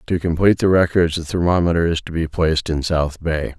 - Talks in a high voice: No, very low, 85 Hz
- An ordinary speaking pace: No, fast, 220 wpm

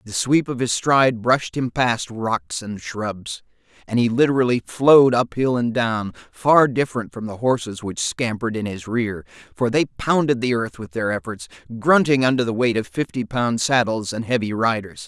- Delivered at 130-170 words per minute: No, average, 185 wpm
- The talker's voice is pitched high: No, low, 115 Hz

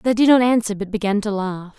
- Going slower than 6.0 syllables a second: Yes, 5.7 syllables/s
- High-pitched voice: Yes, high, 215 Hz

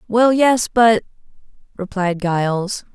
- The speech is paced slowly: Yes, slow, 80 wpm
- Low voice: No, high, 205 Hz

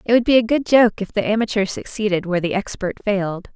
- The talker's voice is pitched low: No, high, 205 Hz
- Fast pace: Yes, fast, 235 wpm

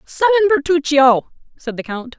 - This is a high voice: Yes, very high, 300 Hz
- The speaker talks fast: No, slow, 135 wpm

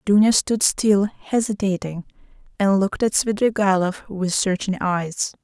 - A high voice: Yes, high, 200 Hz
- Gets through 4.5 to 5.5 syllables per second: No, 4.3 syllables/s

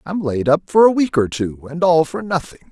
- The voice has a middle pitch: Yes, medium, 160 Hz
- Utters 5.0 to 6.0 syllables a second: Yes, 5.2 syllables/s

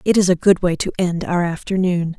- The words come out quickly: Yes, fast, 245 wpm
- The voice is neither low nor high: Yes, medium, 180 Hz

